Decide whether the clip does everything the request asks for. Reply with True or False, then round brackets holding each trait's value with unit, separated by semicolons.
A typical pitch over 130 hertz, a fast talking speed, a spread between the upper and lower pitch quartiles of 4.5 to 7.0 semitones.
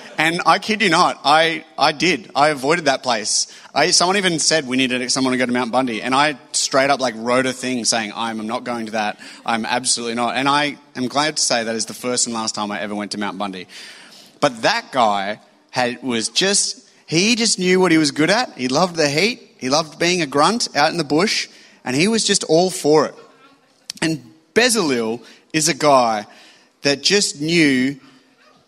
True (140 Hz; 215 wpm; 5.6 semitones)